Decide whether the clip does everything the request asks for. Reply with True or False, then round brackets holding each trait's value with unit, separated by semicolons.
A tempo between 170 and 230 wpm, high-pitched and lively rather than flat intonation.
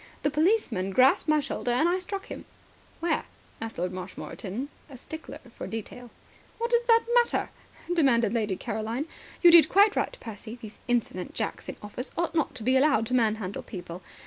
True (175 wpm; 245 Hz; 6.6 semitones)